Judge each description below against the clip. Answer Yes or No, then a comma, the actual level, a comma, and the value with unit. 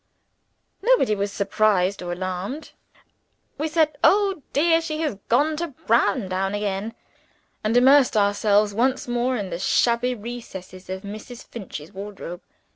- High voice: Yes, high, 215 Hz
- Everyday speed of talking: No, slow, 130 wpm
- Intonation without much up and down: No, average, 5.3 semitones